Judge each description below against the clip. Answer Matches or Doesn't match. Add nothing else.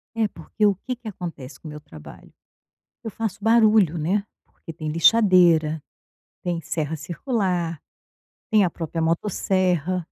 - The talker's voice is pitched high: Doesn't match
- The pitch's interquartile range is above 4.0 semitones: Matches